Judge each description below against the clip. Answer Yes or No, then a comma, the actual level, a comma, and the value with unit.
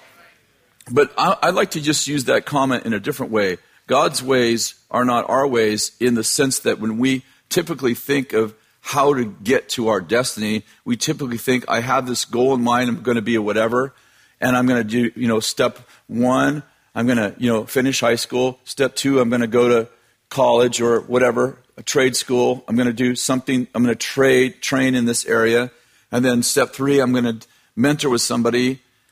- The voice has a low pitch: Yes, low, 125 Hz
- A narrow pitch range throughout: Yes, narrow, 1.8 semitones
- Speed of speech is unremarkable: Yes, average, 195 wpm